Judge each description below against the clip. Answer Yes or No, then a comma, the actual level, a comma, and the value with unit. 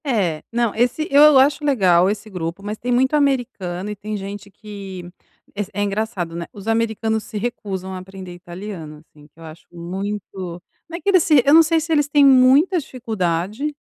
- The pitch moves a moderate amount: No, wide, 6.0 semitones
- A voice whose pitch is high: Yes, high, 210 Hz